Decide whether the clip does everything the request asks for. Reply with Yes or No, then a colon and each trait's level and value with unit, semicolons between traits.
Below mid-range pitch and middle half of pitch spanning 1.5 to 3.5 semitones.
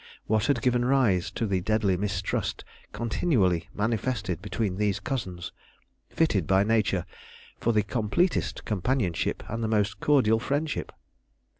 No: low, 110 Hz; average, 4.1 semitones